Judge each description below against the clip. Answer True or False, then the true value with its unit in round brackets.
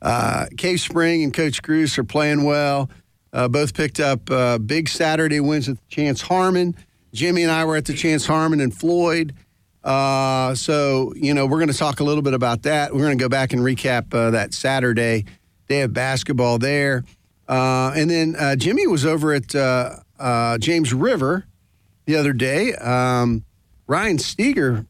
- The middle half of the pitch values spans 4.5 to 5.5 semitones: False (3.7 semitones)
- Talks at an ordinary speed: True (180 wpm)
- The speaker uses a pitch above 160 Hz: False (135 Hz)